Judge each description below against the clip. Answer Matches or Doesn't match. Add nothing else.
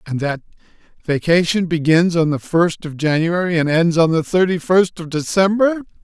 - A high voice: Doesn't match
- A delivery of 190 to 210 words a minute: Doesn't match